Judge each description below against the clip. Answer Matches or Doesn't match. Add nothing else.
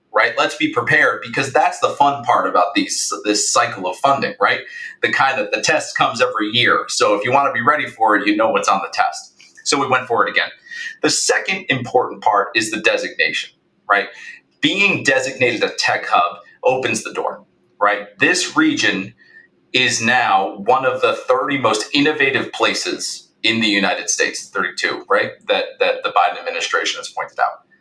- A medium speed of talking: Matches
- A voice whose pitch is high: Matches